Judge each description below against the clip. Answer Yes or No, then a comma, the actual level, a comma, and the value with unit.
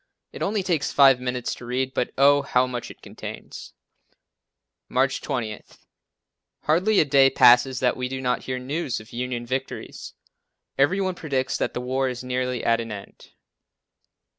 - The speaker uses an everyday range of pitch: No, narrow, 2.0 semitones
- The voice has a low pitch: Yes, low, 130 Hz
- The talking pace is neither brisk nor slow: Yes, average, 165 wpm